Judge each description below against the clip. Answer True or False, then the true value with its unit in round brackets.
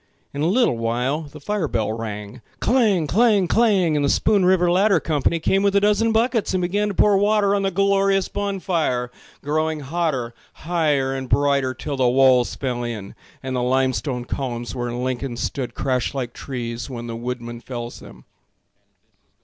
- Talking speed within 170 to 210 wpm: True (175 wpm)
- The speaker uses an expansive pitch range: True (7.8 semitones)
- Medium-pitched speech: True (145 Hz)